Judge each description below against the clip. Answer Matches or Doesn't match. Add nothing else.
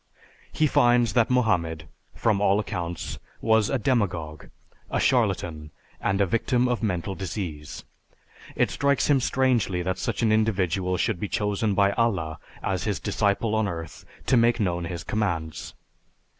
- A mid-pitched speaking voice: Doesn't match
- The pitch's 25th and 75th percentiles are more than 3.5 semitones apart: Matches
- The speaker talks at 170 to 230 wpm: Doesn't match